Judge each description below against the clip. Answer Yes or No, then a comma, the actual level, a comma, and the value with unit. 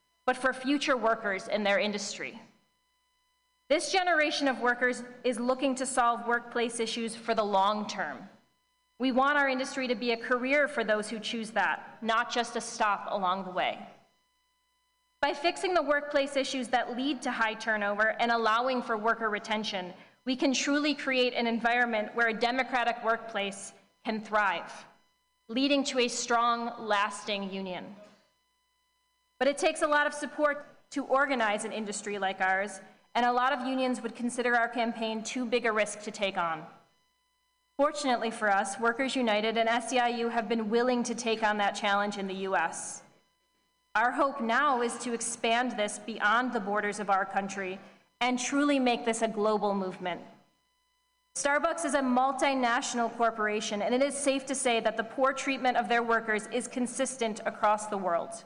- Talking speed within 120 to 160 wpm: No, average, 170 wpm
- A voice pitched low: No, high, 235 Hz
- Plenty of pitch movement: No, average, 4.1 semitones